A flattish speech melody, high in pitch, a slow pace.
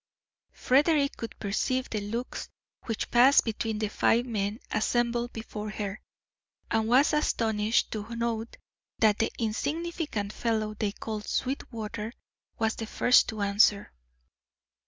Yes: narrow, 2.2 semitones; high, 225 Hz; slow, 125 wpm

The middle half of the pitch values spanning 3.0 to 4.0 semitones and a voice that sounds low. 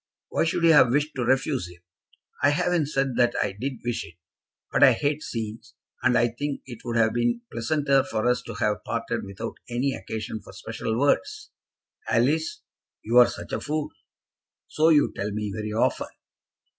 No: average, 4.4 semitones; low, 125 Hz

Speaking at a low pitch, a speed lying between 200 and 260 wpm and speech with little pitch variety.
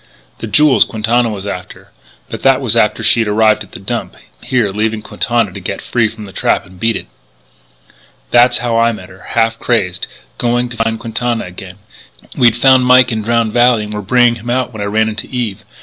Yes: low, 115 Hz; fast, 205 wpm; narrow, 2.3 semitones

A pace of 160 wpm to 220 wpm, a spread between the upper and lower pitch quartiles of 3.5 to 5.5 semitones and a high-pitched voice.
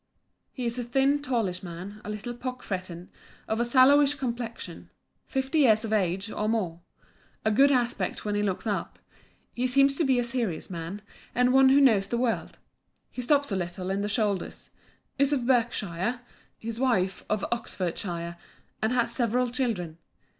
Yes: average, 170 wpm; average, 4.6 semitones; high, 230 Hz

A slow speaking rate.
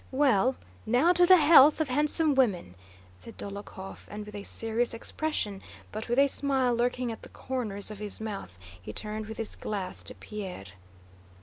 No: average, 175 wpm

